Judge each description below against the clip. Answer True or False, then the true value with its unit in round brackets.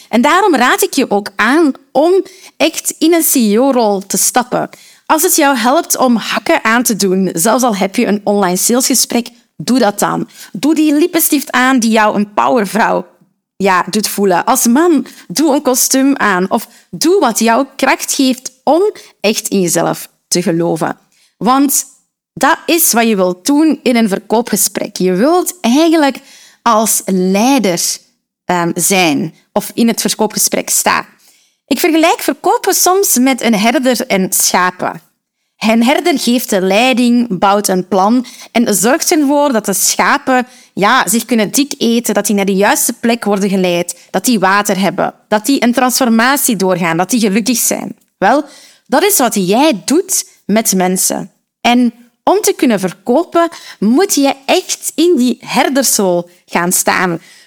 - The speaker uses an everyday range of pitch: False (5.8 semitones)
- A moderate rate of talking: True (160 wpm)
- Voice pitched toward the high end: True (235 Hz)